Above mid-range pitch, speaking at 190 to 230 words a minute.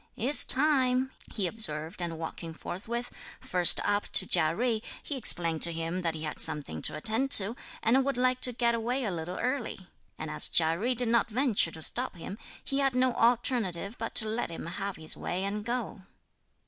Yes: high, 215 Hz; average, 200 wpm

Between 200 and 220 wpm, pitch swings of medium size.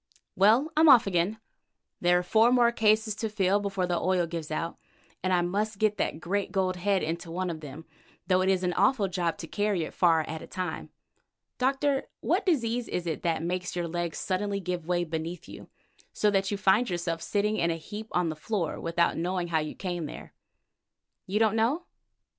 Yes: fast, 205 wpm; average, 3.8 semitones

